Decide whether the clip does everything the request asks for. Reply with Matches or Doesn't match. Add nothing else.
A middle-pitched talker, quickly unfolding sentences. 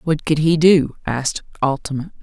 Doesn't match